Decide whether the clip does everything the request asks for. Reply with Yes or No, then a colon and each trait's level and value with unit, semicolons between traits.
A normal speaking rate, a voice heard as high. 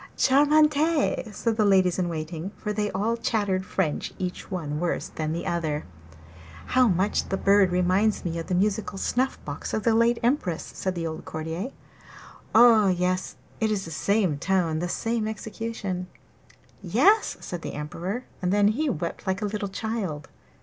Yes: average, 170 wpm; high, 195 Hz